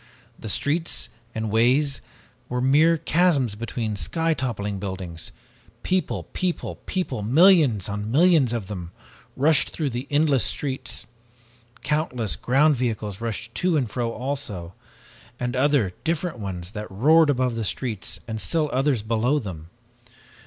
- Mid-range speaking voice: No, low, 125 Hz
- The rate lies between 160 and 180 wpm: No, average, 140 wpm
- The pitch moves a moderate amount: No, wide, 5.9 semitones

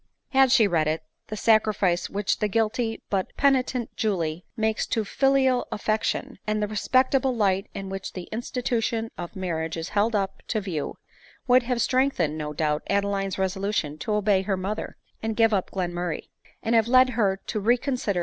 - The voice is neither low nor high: No, high, 210 Hz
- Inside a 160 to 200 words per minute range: Yes, average, 180 wpm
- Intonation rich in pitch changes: No, average, 3.7 semitones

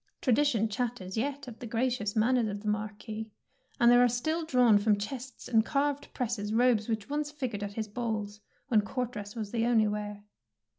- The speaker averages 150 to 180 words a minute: No, average, 200 wpm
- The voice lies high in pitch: Yes, high, 225 Hz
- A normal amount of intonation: Yes, average, 3.1 semitones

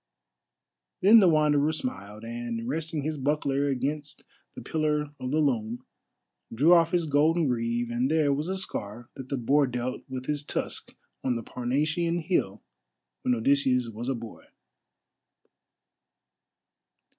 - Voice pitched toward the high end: No, medium, 140 Hz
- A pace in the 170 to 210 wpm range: No, average, 140 wpm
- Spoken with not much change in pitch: No, average, 4.2 semitones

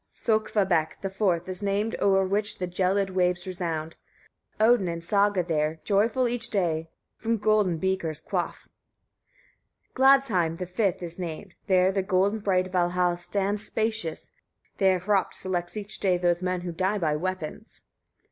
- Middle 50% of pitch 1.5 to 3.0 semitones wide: Yes, average, 2.7 semitones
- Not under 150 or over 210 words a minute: Yes, average, 155 wpm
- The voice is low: No, medium, 185 Hz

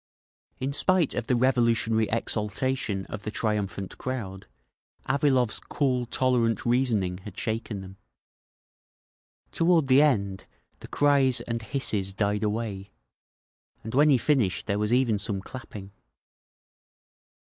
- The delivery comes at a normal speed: No, slow, 120 wpm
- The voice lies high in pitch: No, low, 115 Hz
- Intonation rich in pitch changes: No, average, 4.1 semitones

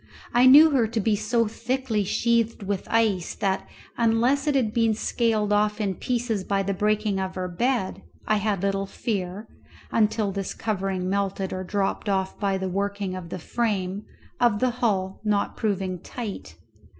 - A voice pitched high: Yes, high, 205 Hz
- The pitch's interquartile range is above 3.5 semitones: No, average, 3.0 semitones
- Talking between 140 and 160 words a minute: No, average, 170 wpm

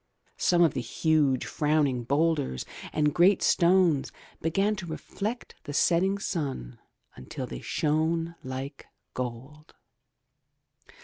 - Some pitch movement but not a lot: Yes, average, 4.3 semitones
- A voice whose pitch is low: No, medium, 155 Hz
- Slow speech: Yes, slow, 110 wpm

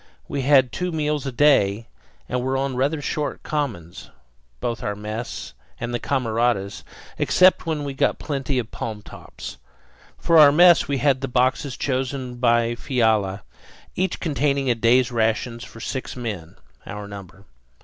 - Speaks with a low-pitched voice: Yes, low, 125 Hz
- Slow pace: No, average, 155 wpm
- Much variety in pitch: No, average, 3.8 semitones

